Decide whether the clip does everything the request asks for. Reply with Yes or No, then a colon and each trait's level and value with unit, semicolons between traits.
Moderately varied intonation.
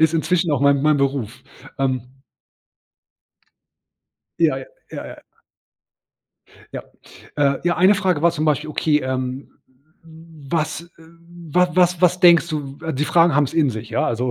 Yes: average, 3.6 semitones